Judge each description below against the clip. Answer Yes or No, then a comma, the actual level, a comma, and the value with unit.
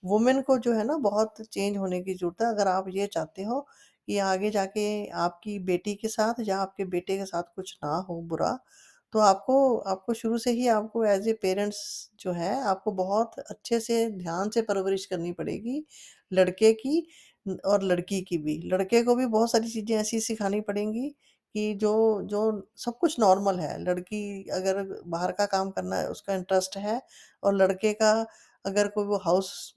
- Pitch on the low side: No, high, 205 Hz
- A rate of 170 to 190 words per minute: Yes, average, 185 wpm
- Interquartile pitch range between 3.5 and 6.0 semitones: No, average, 2.8 semitones